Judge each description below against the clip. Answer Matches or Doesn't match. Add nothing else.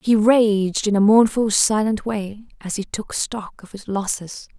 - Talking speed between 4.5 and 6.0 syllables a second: Doesn't match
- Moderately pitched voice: Doesn't match